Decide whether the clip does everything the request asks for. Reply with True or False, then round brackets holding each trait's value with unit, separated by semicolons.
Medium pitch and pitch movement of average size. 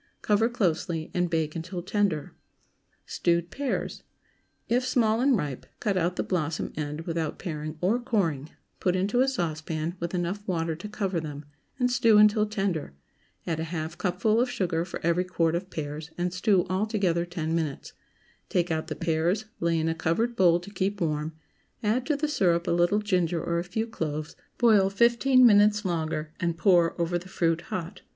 True (175 Hz; 4.3 semitones)